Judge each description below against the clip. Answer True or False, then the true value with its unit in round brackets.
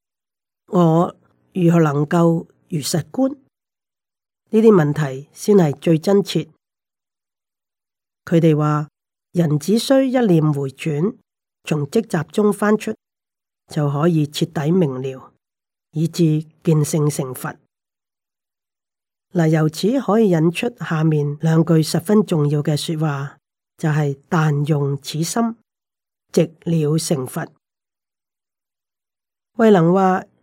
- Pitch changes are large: False (3.7 semitones)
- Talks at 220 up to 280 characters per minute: False (155 characters per minute)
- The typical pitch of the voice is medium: True (165 Hz)